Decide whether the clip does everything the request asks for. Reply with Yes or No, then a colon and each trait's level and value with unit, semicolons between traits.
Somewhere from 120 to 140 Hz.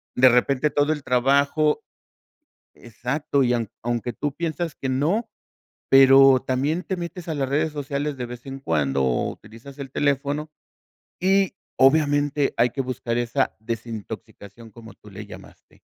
Yes: low, 135 Hz